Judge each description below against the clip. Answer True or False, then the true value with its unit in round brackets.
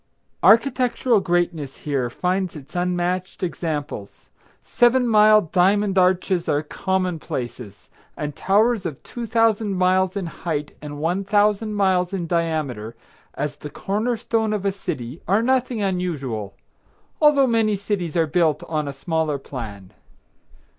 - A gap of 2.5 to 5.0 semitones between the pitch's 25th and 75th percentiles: False (5.6 semitones)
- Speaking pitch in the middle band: True (180 Hz)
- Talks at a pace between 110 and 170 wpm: True (135 wpm)